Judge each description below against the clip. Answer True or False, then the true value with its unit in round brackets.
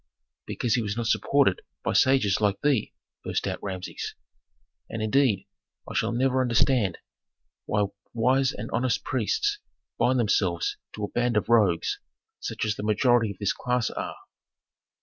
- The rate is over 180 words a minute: False (150 wpm)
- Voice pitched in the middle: False (115 Hz)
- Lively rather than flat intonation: False (3.7 semitones)